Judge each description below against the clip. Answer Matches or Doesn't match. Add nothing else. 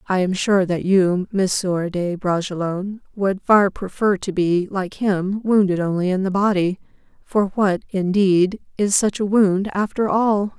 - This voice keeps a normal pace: Matches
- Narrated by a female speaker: Matches